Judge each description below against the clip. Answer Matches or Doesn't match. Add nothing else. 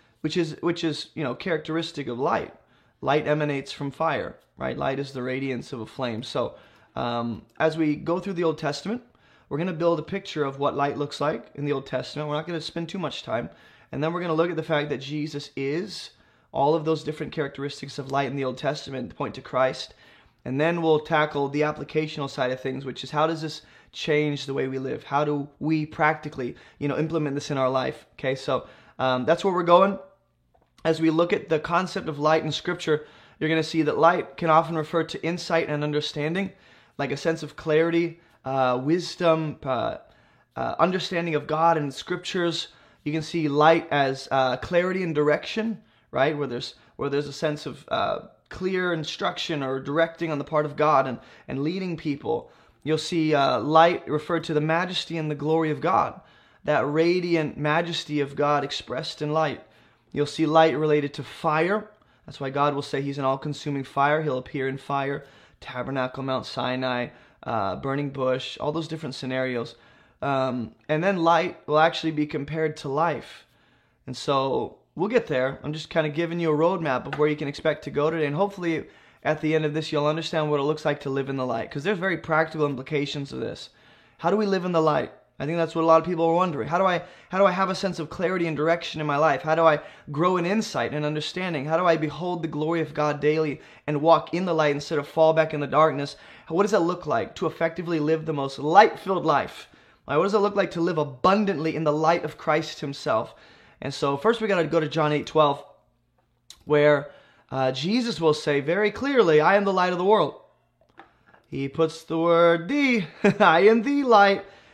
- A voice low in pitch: Doesn't match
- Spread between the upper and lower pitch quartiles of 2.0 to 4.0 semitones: Matches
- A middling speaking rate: Doesn't match